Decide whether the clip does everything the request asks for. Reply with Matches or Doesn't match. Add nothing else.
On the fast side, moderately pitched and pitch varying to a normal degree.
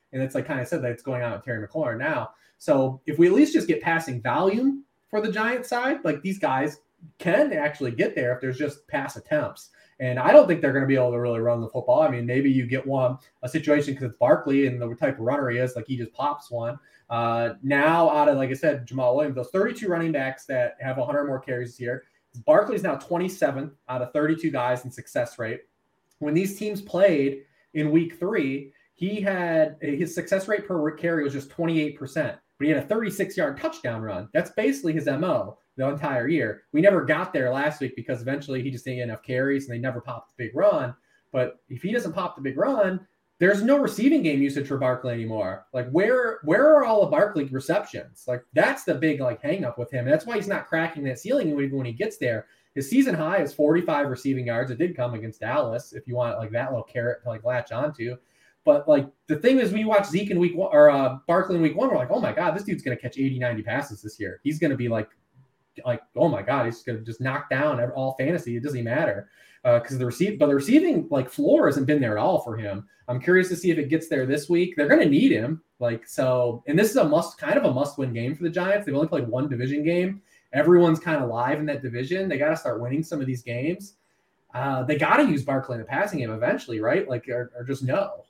Doesn't match